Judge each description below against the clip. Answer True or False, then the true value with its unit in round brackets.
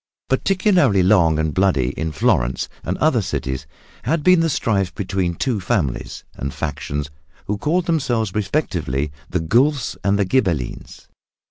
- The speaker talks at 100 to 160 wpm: True (140 wpm)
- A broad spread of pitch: True (8.9 semitones)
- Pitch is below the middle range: True (95 Hz)